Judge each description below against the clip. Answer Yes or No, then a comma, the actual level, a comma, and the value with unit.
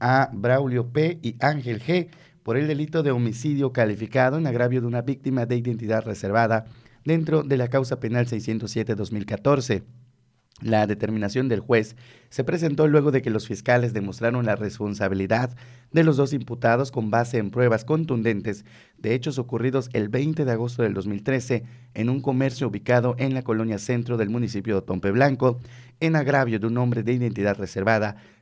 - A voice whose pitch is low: Yes, low, 120 Hz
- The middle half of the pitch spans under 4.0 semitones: Yes, average, 3.2 semitones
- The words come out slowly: No, average, 165 wpm